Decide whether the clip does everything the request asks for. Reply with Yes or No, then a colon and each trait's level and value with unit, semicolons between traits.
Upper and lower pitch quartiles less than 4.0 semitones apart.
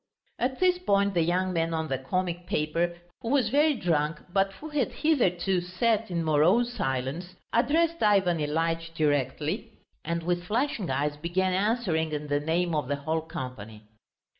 No: average, 5.2 semitones